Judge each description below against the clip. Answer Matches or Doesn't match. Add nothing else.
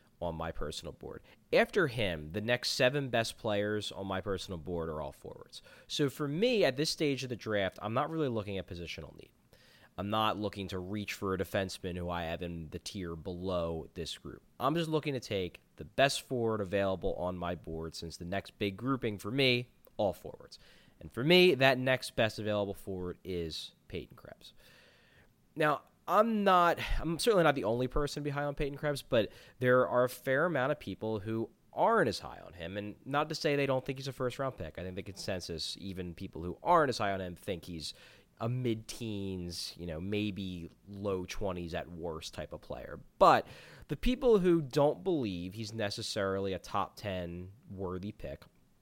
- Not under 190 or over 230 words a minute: Matches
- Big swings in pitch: Matches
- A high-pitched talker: Doesn't match